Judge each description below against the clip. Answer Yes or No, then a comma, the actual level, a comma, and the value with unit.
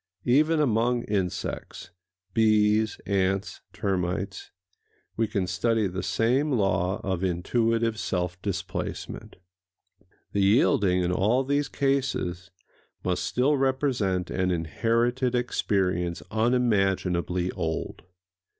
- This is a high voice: No, low, 100 Hz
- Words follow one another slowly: Yes, slow, 90 wpm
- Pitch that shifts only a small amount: No, average, 4.6 semitones